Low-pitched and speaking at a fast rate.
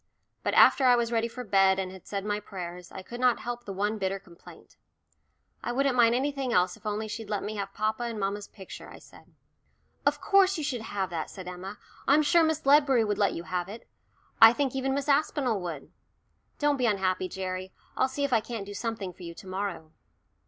No: high, 215 Hz; fast, 220 wpm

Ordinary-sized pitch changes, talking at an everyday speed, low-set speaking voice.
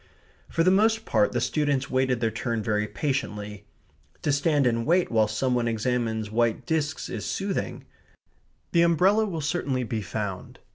No: wide, 6.4 semitones; average, 160 wpm; low, 125 Hz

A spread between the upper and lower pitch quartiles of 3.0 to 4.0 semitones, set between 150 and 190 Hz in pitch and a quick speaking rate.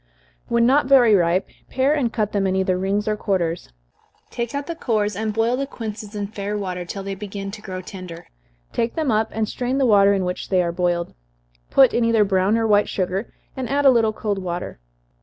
No: average, 3.6 semitones; high, 210 Hz; fast, 215 wpm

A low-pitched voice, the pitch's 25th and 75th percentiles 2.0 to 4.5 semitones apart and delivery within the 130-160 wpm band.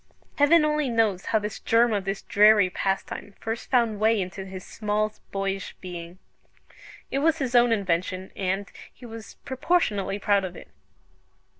No: high, 210 Hz; average, 3.5 semitones; average, 155 wpm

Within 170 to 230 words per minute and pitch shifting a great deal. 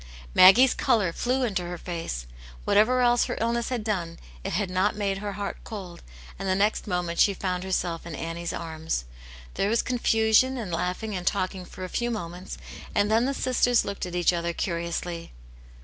No: average, 185 wpm; average, 4.1 semitones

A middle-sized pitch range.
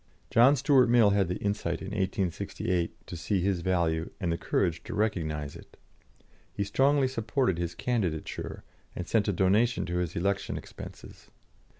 Yes: average, 4.5 semitones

